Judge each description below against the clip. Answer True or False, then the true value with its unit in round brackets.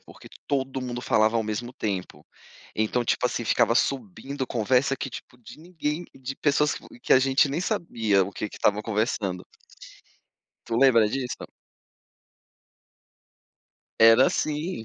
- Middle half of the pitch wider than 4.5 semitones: False (3.8 semitones)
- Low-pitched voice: True (125 Hz)